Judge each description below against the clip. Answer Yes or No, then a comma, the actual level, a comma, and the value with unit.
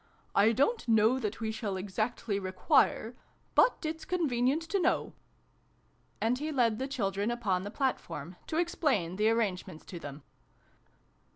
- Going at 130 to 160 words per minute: Yes, average, 150 wpm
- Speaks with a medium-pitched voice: No, high, 225 Hz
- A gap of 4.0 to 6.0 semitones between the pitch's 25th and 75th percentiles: Yes, wide, 5.5 semitones